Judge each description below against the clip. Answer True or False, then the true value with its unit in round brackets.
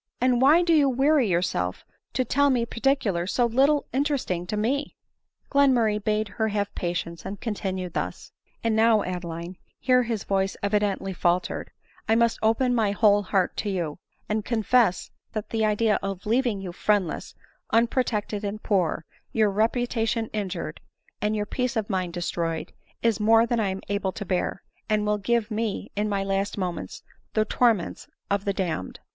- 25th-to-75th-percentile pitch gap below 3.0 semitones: False (3.4 semitones)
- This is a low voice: False (210 Hz)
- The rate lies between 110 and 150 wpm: False (175 wpm)